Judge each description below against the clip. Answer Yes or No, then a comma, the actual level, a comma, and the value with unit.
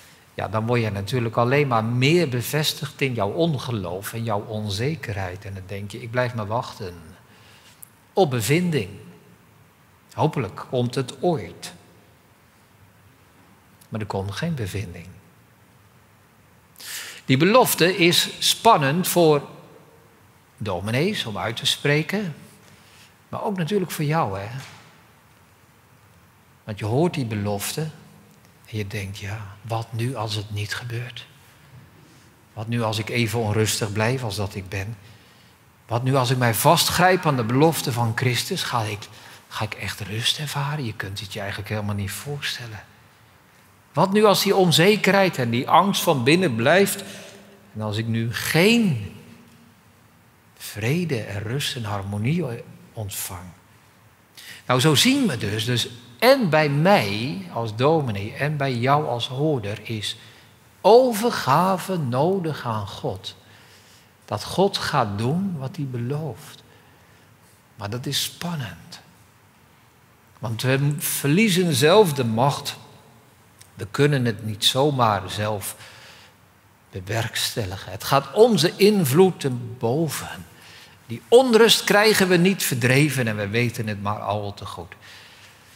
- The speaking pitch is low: Yes, low, 120 Hz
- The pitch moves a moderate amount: No, wide, 5.8 semitones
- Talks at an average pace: No, slow, 130 wpm